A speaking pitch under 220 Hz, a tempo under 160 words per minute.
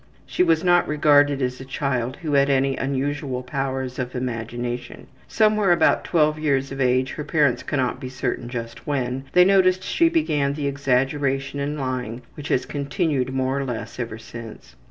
No: low, 135 Hz; average, 175 wpm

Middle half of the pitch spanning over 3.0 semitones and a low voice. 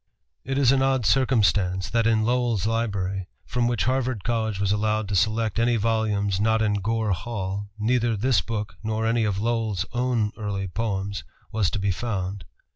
No: average, 2.7 semitones; low, 110 Hz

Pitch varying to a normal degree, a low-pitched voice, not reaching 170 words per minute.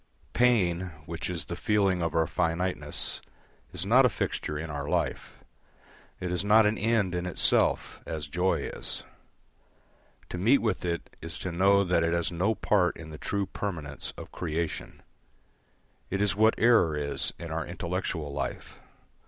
Yes: average, 3.4 semitones; very low, 90 Hz; average, 160 wpm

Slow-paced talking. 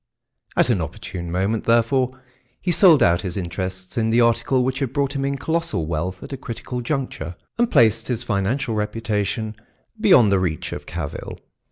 No: average, 175 wpm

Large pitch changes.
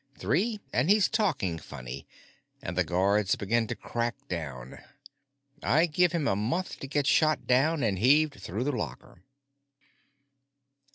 Yes: wide, 8.5 semitones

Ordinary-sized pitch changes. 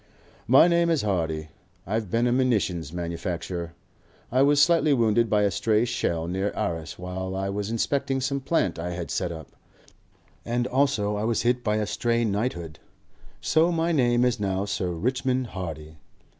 No: wide, 6.0 semitones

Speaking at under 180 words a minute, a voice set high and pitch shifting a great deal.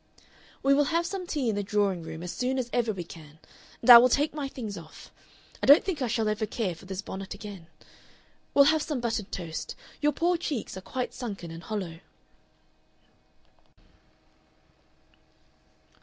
Yes: average, 170 wpm; high, 225 Hz; wide, 6.6 semitones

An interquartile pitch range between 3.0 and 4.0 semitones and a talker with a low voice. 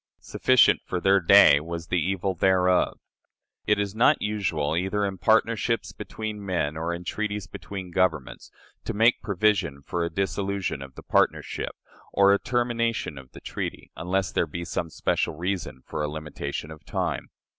Yes: average, 3.7 semitones; very low, 95 Hz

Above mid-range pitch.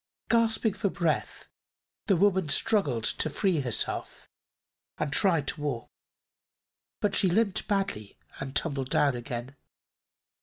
No: medium, 165 Hz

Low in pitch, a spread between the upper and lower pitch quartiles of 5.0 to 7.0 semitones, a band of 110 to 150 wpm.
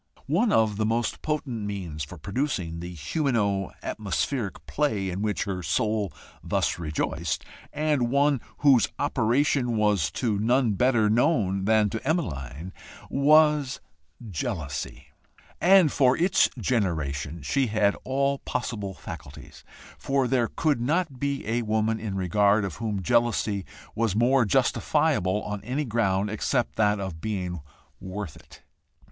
Yes: low, 110 Hz; wide, 5.5 semitones; slow, 135 wpm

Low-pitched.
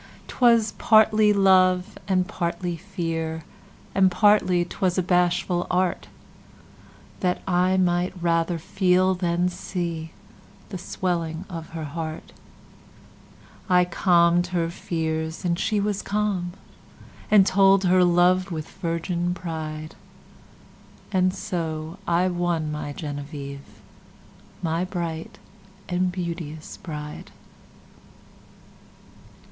No: medium, 175 Hz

